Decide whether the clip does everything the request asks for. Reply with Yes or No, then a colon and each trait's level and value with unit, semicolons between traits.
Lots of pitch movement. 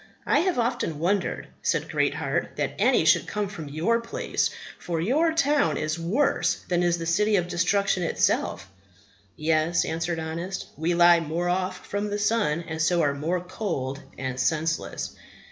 No: average, 4.1 semitones